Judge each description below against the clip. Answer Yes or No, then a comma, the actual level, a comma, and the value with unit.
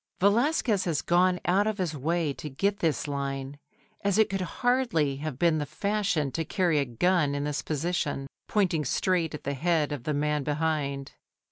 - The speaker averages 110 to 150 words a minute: No, average, 180 wpm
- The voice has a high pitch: No, medium, 160 Hz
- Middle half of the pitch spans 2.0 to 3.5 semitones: No, average, 4.4 semitones